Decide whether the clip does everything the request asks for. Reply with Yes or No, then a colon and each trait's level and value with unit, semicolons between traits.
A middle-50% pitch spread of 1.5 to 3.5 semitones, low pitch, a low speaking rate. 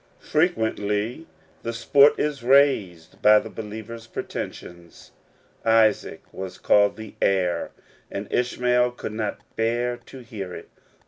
Yes: average, 3.2 semitones; low, 110 Hz; slow, 120 wpm